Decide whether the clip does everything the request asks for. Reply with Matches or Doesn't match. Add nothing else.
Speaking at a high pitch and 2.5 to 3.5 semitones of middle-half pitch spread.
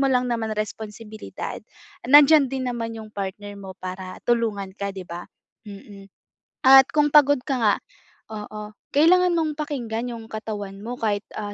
Doesn't match